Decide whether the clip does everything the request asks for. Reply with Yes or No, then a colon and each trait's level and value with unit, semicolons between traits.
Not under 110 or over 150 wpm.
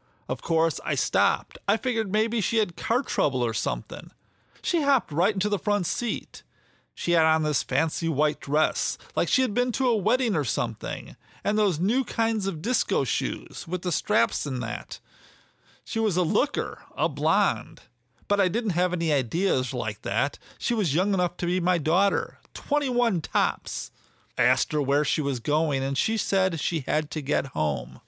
No: average, 185 wpm